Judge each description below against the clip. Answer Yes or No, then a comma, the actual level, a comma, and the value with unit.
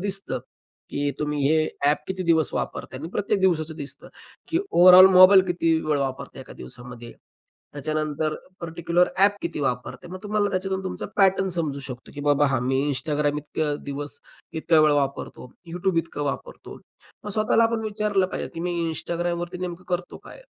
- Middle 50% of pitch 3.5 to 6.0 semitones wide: Yes, average, 4.2 semitones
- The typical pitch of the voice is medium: Yes, medium, 165 Hz